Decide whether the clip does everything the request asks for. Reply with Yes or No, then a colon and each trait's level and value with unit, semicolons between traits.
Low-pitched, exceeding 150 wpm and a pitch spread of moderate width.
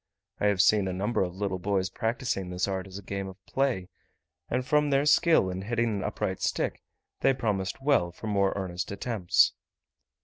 Yes: low, 100 Hz; average, 190 wpm; average, 4.1 semitones